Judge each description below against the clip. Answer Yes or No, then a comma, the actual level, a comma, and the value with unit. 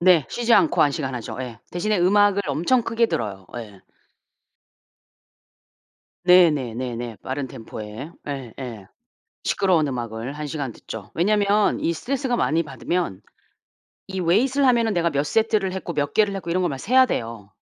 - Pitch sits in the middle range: Yes, medium, 165 Hz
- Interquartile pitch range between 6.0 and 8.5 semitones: Yes, wide, 8.2 semitones